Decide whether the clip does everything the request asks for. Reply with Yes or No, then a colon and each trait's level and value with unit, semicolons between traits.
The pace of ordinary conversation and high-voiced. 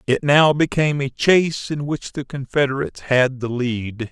No: average, 175 wpm; low, 135 Hz